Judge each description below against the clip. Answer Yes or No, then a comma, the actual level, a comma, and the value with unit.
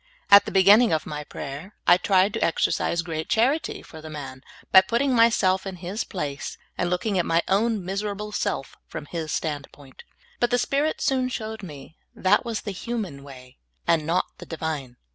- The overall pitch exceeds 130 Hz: Yes, medium, 185 Hz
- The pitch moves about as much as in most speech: No, wide, 5.8 semitones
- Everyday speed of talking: Yes, average, 180 wpm